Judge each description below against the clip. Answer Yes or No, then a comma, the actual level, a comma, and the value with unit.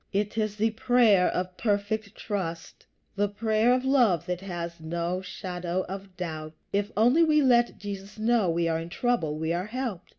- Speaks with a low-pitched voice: No, high, 200 Hz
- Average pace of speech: Yes, average, 175 wpm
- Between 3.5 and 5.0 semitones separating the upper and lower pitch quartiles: Yes, average, 4.2 semitones